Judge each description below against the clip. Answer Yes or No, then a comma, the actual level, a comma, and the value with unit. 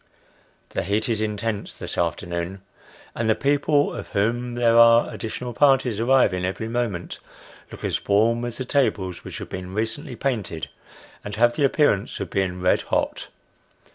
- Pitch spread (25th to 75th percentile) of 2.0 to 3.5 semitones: No, average, 3.9 semitones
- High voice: No, low, 115 Hz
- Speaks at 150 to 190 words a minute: Yes, average, 160 wpm